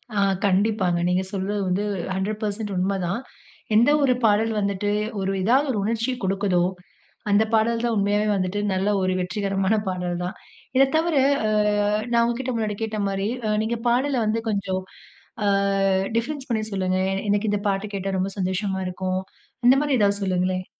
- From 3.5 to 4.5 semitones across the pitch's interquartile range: No, average, 2.9 semitones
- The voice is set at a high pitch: Yes, high, 205 Hz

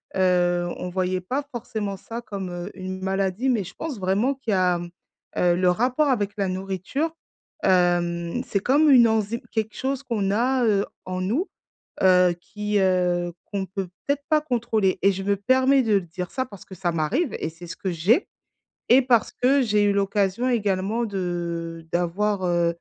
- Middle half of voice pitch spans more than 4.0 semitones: Yes, average, 4.7 semitones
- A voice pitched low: No, high, 195 Hz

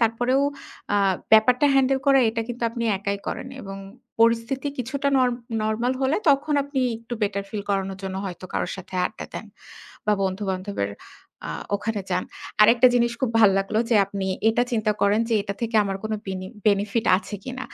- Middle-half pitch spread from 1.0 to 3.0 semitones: No, average, 3.6 semitones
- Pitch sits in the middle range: No, high, 220 Hz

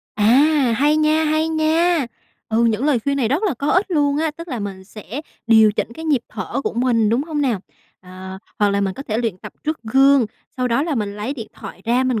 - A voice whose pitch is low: No, very high, 255 Hz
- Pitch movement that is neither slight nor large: No, wide, 5.7 semitones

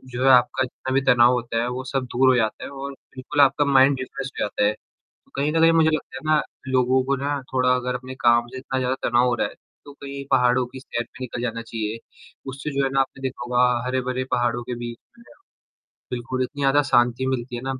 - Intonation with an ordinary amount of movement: No, narrow, 1.8 semitones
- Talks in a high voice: No, low, 130 Hz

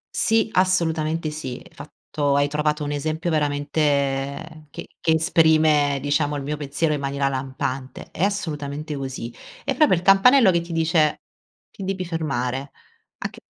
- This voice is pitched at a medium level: Yes, medium, 150 Hz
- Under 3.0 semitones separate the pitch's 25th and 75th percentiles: Yes, narrow, 2.6 semitones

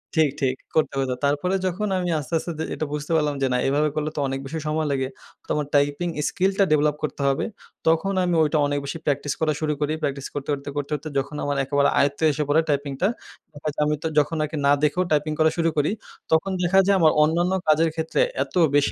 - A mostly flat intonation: Yes, narrow, 2.1 semitones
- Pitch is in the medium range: Yes, medium, 150 Hz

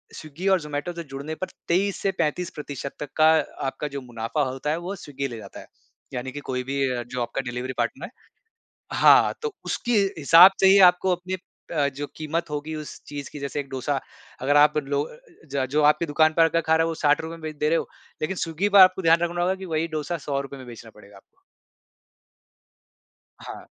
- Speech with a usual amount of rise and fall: Yes, average, 3.4 semitones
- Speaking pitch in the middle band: Yes, medium, 150 Hz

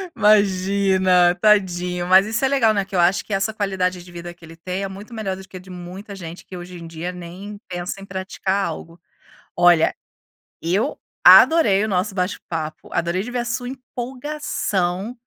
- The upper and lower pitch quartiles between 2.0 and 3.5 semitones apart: Yes, average, 2.9 semitones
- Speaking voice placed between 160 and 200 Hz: Yes, high, 190 Hz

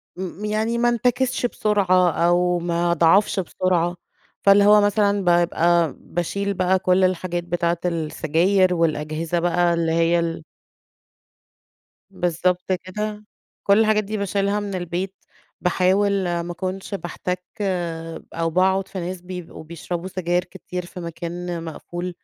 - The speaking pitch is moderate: Yes, medium, 180 Hz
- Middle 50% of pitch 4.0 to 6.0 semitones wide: No, narrow, 2.4 semitones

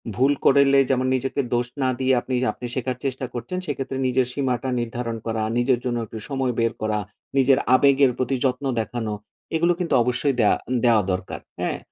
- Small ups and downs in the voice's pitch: Yes, narrow, 2.1 semitones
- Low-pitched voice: Yes, low, 130 Hz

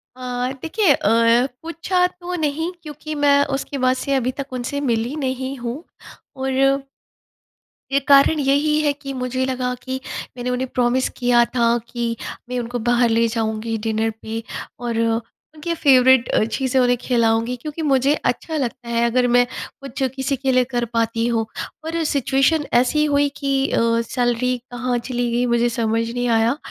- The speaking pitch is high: Yes, very high, 255 Hz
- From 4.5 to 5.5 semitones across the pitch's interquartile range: No, average, 2.8 semitones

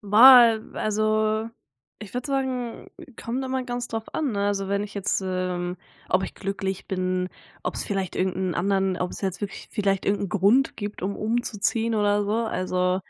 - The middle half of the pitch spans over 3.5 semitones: No, average, 3.1 semitones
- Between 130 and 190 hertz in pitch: No, high, 205 Hz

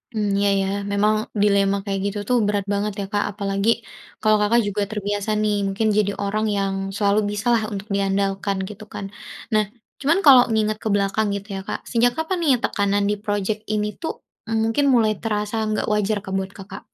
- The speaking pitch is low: No, high, 210 Hz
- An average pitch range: No, narrow, 1.4 semitones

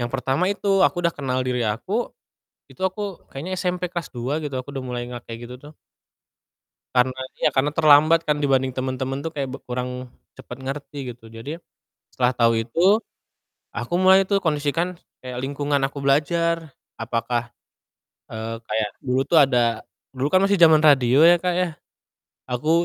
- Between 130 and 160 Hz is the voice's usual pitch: Yes, medium, 140 Hz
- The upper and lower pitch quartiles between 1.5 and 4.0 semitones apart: No, average, 5.0 semitones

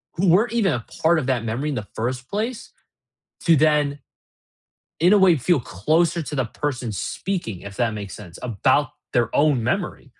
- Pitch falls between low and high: Yes, medium, 145 Hz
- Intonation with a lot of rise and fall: Yes, wide, 6.7 semitones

